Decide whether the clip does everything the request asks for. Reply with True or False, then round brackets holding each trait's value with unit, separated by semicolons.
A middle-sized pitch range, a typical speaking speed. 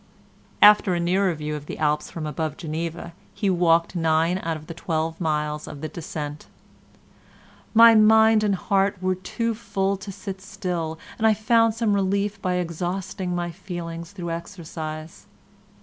True (3.6 semitones; 160 wpm)